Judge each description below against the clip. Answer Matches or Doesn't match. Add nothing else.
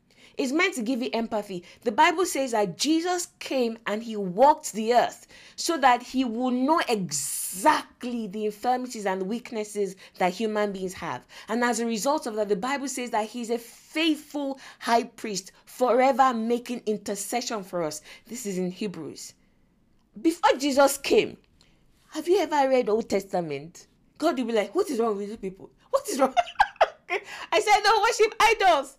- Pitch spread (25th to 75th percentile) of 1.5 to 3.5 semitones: Doesn't match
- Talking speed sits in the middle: Matches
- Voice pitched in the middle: Doesn't match